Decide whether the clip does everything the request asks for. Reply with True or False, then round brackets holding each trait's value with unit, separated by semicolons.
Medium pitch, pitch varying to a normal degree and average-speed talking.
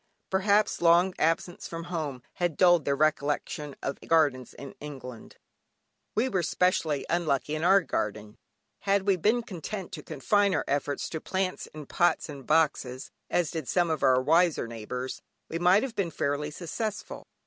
True (160 Hz; 4.3 semitones; 160 wpm)